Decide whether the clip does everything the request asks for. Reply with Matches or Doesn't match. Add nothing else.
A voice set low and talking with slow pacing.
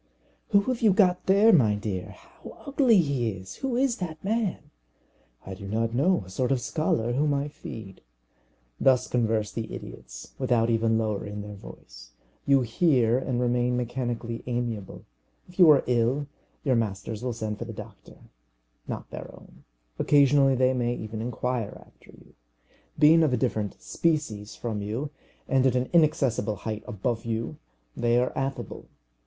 Doesn't match